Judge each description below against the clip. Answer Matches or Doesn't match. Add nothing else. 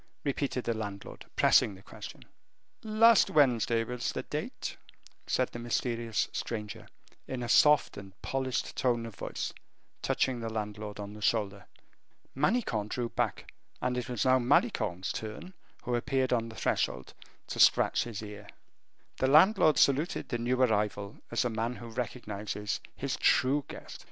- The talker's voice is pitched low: Matches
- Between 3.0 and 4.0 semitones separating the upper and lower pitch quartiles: Matches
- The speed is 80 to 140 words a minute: Doesn't match